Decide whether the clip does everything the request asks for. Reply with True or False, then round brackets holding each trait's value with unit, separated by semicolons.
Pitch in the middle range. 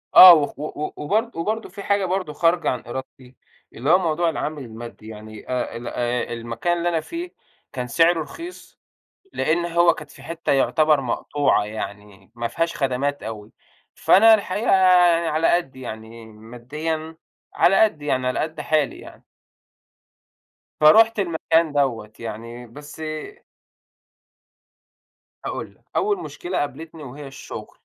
True (150 Hz)